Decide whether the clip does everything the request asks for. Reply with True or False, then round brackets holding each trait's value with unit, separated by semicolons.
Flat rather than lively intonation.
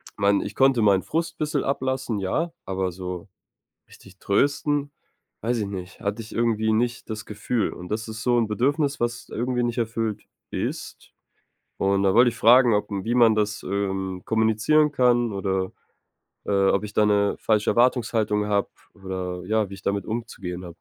False (3.5 semitones)